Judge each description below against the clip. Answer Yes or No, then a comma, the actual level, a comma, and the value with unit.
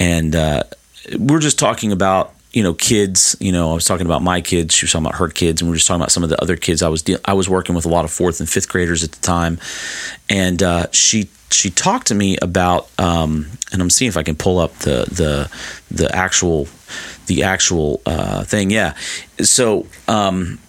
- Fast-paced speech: Yes, fast, 230 wpm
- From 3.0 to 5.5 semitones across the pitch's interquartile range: No, narrow, 2.4 semitones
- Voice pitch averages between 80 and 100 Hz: Yes, very low, 90 Hz